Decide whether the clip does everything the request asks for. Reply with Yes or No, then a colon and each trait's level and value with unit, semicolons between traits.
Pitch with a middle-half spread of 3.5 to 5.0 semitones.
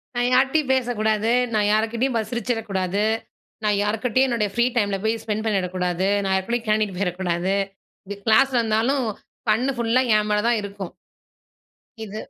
No: average, 3.0 semitones